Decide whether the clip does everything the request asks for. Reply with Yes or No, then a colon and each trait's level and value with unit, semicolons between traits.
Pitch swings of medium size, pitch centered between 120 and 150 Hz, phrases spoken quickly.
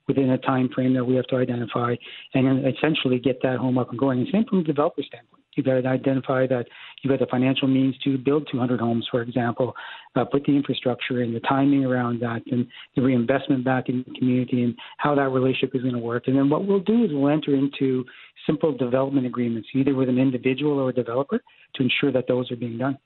No: narrow, 1.6 semitones; low, 130 Hz; fast, 235 wpm